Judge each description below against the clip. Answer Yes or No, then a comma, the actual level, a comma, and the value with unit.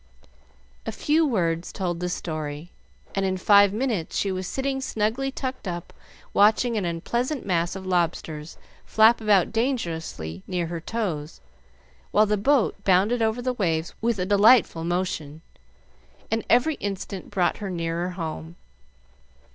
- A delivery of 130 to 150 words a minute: Yes, average, 140 wpm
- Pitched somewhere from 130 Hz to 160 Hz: No, high, 190 Hz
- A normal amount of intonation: Yes, average, 4.9 semitones